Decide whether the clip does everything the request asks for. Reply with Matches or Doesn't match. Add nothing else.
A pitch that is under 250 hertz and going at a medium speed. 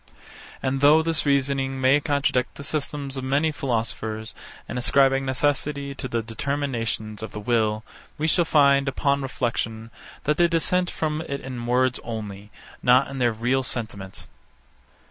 Matches